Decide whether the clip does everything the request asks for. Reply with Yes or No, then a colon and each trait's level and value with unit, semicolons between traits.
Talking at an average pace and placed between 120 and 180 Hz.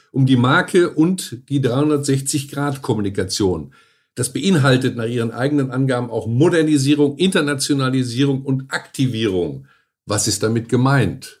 No: slow, 110 wpm; low, 135 Hz